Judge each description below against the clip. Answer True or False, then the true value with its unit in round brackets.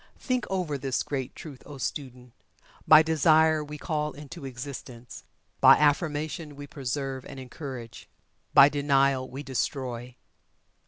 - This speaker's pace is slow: True (125 wpm)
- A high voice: False (140 Hz)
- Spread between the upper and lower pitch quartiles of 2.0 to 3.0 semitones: True (2.6 semitones)